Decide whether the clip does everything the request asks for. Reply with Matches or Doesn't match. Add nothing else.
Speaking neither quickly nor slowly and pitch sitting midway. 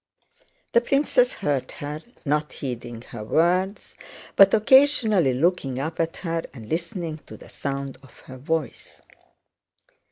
Doesn't match